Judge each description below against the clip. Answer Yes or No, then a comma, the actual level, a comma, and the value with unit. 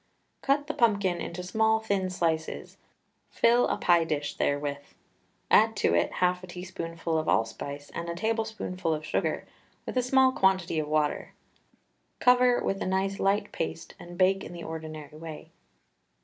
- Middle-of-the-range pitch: Yes, medium, 180 Hz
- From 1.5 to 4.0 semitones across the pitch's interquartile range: No, average, 4.4 semitones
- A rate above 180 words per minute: No, average, 160 wpm